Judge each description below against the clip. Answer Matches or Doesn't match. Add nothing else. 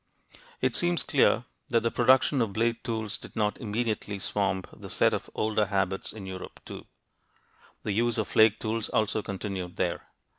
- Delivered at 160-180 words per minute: Matches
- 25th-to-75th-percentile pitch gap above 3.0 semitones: Doesn't match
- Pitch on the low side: Matches